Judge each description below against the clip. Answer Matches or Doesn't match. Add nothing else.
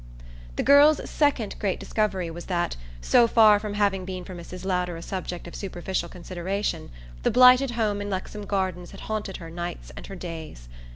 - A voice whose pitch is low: Doesn't match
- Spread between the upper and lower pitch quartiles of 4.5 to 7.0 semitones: Doesn't match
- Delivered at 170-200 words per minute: Matches